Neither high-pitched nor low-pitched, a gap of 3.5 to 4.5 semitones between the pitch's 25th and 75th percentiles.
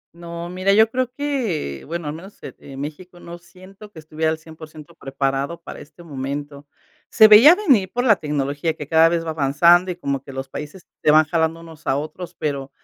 Yes: medium, 160 Hz; average, 4.0 semitones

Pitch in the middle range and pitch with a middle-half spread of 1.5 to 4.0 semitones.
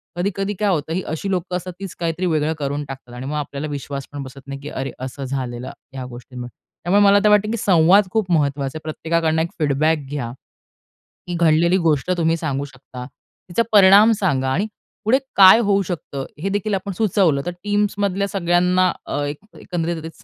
No: medium, 165 Hz; wide, 5.6 semitones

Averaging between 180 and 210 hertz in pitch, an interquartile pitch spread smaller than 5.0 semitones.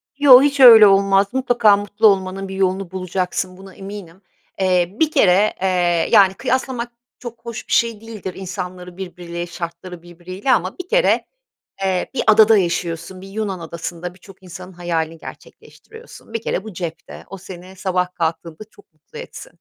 Yes: high, 190 Hz; average, 3.5 semitones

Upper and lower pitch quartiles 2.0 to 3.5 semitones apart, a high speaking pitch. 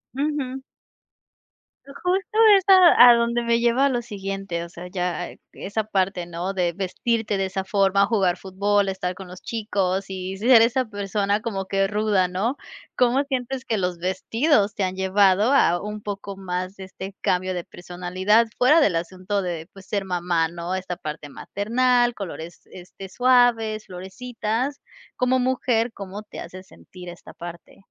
No: average, 4.2 semitones; high, 200 Hz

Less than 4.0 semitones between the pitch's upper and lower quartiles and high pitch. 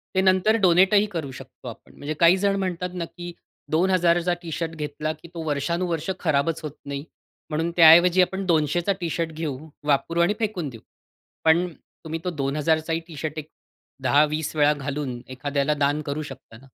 No: average, 3.0 semitones; medium, 160 Hz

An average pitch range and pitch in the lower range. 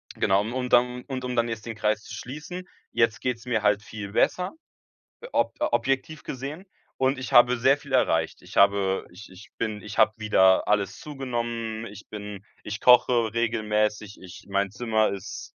Yes: average, 3.3 semitones; low, 115 Hz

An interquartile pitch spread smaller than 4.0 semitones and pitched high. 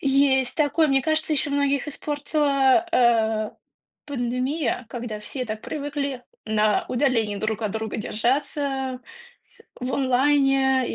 Yes: average, 3.3 semitones; very high, 265 Hz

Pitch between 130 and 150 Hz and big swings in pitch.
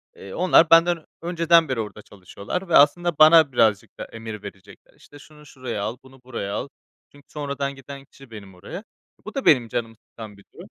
Yes: low, 135 Hz; wide, 6.6 semitones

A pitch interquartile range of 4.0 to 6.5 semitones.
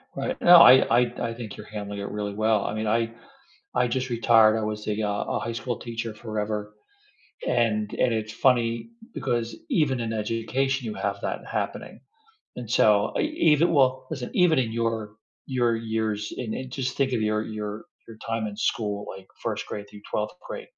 No: narrow, 2.5 semitones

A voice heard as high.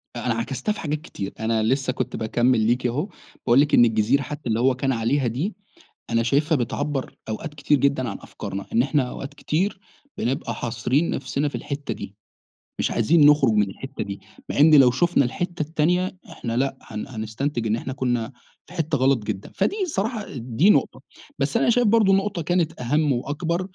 No: low, 135 Hz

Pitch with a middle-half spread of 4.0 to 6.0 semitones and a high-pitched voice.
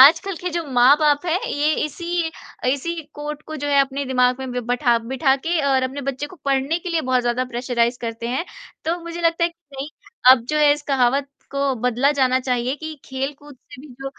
No: average, 3.3 semitones; very high, 275 Hz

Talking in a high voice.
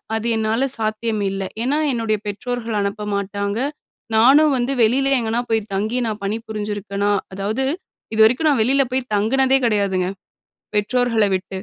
Yes: high, 220 Hz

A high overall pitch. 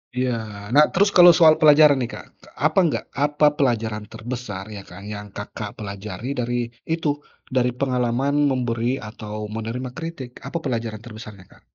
No: low, 120 Hz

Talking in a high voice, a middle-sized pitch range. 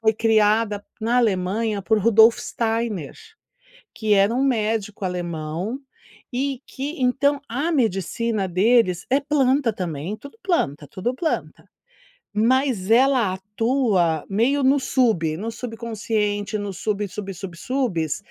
Yes: high, 220 Hz; average, 4.4 semitones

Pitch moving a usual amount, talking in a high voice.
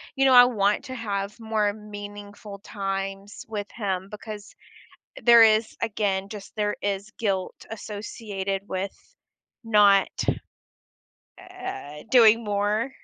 No: narrow, 1.8 semitones; high, 205 Hz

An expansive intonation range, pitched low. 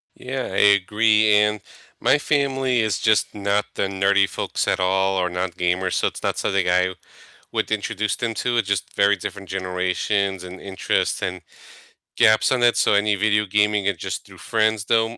No: narrow, 2.4 semitones; low, 100 Hz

